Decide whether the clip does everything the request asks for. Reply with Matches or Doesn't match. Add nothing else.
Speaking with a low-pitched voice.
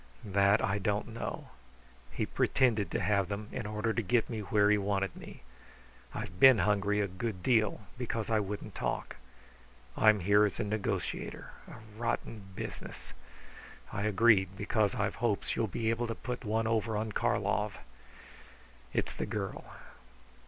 Matches